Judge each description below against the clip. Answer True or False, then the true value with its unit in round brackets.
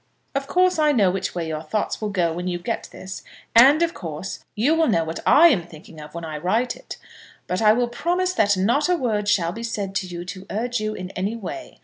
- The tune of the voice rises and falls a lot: True (5.8 semitones)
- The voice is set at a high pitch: True (205 Hz)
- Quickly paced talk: True (245 wpm)